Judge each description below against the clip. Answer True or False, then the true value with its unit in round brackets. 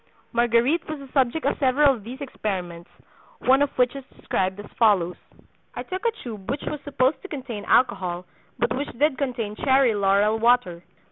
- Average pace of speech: True (180 wpm)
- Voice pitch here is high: True (245 Hz)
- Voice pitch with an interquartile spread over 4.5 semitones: True (5.0 semitones)